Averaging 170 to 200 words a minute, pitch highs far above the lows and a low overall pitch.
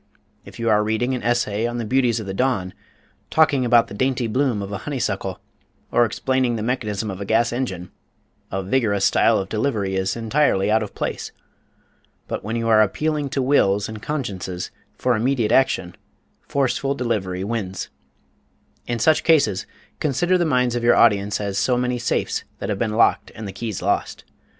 No: average, 185 wpm; average, 4.0 semitones; low, 115 Hz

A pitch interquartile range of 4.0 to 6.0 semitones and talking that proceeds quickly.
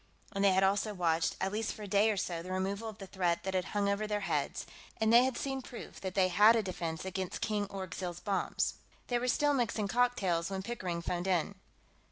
No: average, 2.8 semitones; fast, 230 wpm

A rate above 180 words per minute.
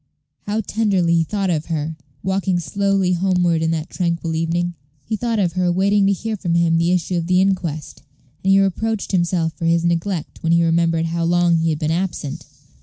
Yes: average, 200 wpm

